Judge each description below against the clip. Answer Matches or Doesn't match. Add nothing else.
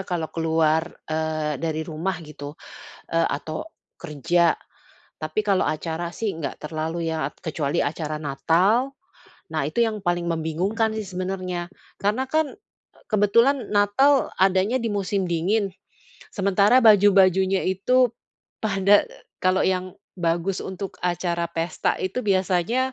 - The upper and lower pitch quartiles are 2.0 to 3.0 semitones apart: Doesn't match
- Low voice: Doesn't match